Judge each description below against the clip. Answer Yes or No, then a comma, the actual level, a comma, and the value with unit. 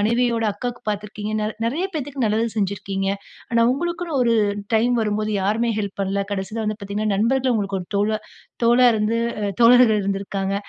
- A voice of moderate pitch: No, high, 215 Hz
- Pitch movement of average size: Yes, average, 3.1 semitones